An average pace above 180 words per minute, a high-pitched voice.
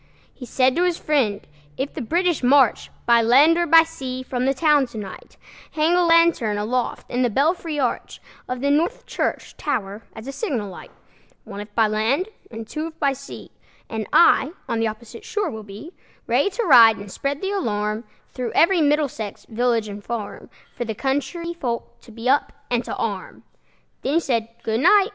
Yes: average, 190 wpm; very high, 255 Hz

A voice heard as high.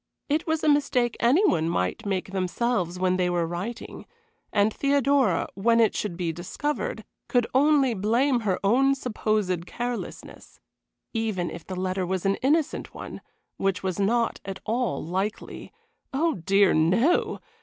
Yes: high, 215 Hz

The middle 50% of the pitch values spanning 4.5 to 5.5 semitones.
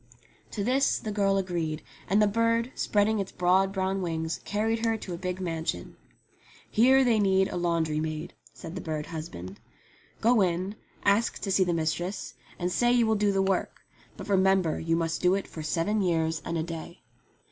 No: average, 3.8 semitones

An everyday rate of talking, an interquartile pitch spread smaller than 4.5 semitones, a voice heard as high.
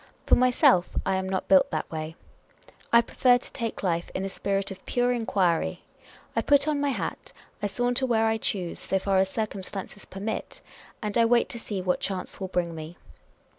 Yes: average, 195 wpm; average, 4.0 semitones; high, 195 Hz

